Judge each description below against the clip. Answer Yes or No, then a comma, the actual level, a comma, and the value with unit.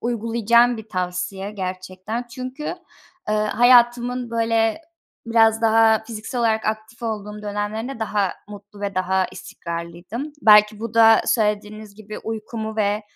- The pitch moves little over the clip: Yes, narrow, 1.9 semitones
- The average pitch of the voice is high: Yes, high, 220 Hz